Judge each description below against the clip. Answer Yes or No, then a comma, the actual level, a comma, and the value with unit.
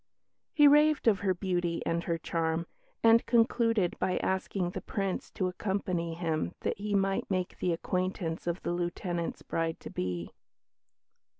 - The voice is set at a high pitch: No, medium, 180 Hz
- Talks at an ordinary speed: Yes, average, 155 wpm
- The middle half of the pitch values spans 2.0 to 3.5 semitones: Yes, average, 3.0 semitones